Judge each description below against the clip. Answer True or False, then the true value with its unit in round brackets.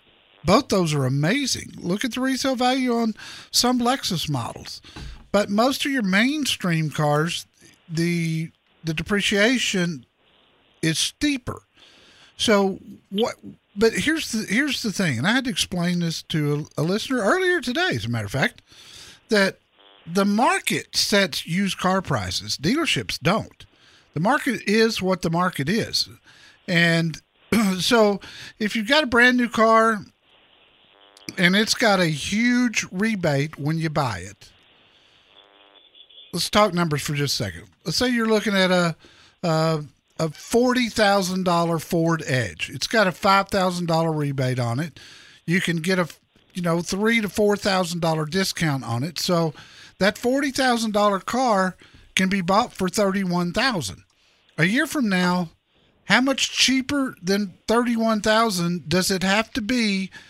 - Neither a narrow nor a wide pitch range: False (5.8 semitones)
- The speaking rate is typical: True (155 wpm)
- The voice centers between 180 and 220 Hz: True (190 Hz)